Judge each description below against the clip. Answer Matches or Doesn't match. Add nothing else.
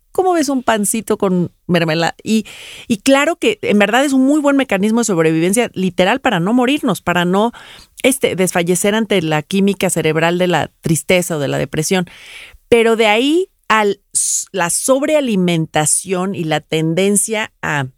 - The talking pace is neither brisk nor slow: Matches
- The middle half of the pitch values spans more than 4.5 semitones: Matches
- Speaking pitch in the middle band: Doesn't match